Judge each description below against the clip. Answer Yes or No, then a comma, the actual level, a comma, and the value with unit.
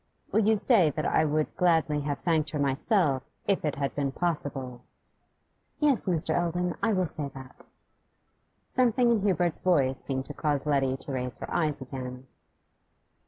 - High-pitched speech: No, medium, 150 Hz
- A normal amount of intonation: Yes, average, 4.7 semitones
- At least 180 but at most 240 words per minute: No, average, 165 wpm